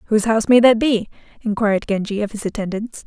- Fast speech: No, average, 195 wpm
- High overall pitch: Yes, high, 215 Hz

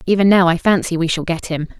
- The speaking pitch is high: No, medium, 175 Hz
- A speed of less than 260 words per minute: No, fast, 270 wpm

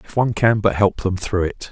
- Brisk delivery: Yes, fast, 280 wpm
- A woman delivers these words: No, male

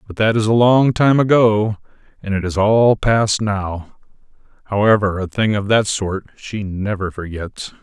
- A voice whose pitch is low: Yes, low, 105 Hz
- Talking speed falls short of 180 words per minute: Yes, average, 170 wpm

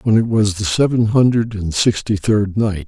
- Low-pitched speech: Yes, low, 105 Hz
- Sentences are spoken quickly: Yes, fast, 210 wpm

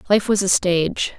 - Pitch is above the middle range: Yes, high, 195 Hz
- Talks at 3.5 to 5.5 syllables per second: Yes, 5.3 syllables/s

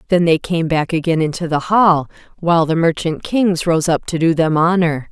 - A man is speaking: No, female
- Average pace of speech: No, fast, 210 wpm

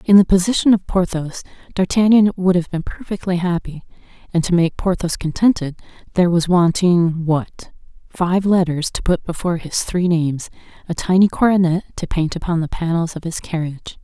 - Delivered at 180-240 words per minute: No, average, 160 wpm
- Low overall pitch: No, medium, 175 Hz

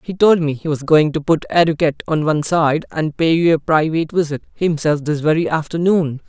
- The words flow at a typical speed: No, fast, 210 wpm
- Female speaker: No, male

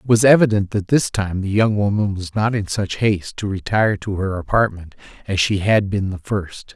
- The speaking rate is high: Yes, fast, 220 wpm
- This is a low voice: Yes, low, 100 Hz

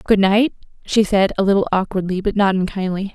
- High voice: Yes, high, 195 Hz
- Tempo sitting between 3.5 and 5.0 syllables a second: No, 5.8 syllables/s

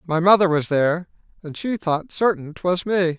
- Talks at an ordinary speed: Yes, average, 190 wpm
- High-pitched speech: No, medium, 175 Hz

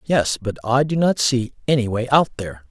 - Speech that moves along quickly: Yes, fast, 220 wpm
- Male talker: Yes, male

